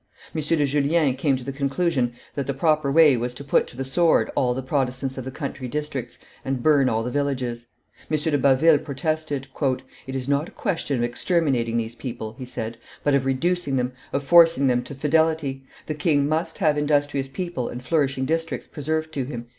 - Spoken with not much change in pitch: No, average, 3.0 semitones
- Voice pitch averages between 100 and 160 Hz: Yes, medium, 140 Hz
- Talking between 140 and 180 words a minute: No, average, 200 wpm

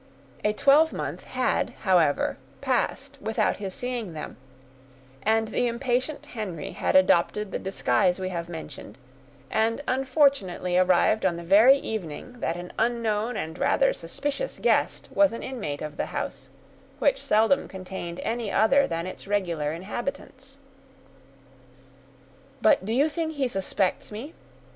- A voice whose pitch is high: Yes, high, 215 Hz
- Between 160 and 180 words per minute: No, slow, 135 wpm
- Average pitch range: No, wide, 6.1 semitones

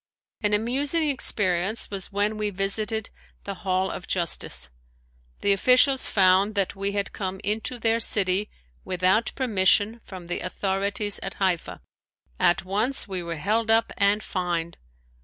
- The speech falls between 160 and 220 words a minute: No, average, 140 wpm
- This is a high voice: Yes, high, 200 Hz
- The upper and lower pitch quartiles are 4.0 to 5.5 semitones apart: No, average, 2.8 semitones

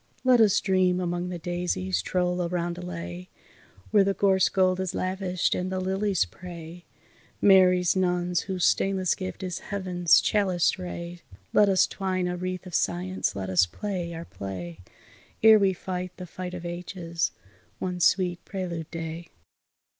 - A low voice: No, medium, 180 Hz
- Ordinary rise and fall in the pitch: No, narrow, 1.5 semitones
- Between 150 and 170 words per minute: Yes, average, 155 wpm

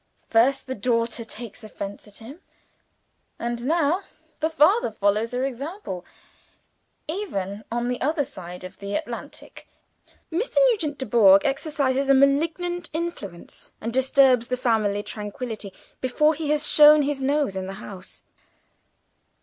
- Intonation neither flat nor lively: No, wide, 5.8 semitones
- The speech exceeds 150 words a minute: No, slow, 135 wpm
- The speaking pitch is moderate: No, very high, 255 Hz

